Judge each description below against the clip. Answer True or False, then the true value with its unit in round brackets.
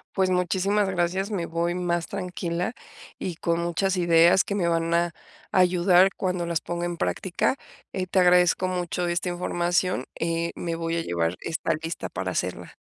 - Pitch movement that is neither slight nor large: False (1.5 semitones)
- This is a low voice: False (175 Hz)